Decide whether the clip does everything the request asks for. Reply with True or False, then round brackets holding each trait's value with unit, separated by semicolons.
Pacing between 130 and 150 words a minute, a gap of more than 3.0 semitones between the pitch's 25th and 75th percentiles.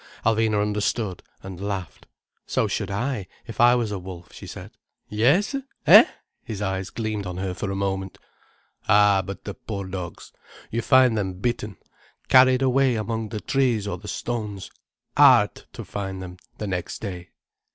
False (160 wpm; 3.4 semitones)